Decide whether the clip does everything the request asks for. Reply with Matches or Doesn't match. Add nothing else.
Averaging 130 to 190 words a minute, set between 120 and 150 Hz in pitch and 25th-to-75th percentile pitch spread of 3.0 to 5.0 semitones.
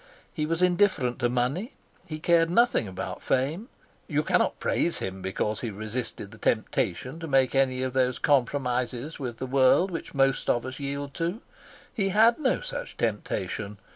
Doesn't match